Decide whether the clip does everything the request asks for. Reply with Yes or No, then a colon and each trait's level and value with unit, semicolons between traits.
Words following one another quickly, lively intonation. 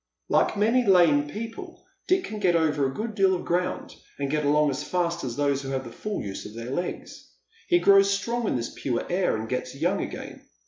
Yes: fast, 220 wpm; wide, 6.6 semitones